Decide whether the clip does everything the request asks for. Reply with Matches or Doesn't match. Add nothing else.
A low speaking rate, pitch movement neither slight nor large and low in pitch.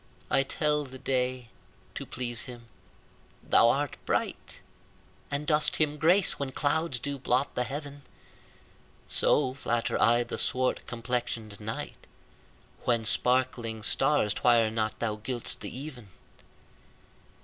Matches